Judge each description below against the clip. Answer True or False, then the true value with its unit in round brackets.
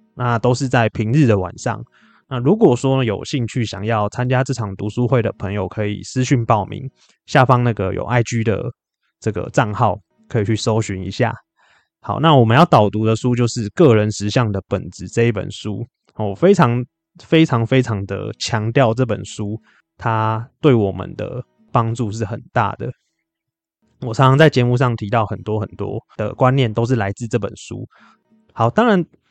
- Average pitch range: True (3.6 semitones)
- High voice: False (115 Hz)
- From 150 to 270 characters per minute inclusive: True (255 characters per minute)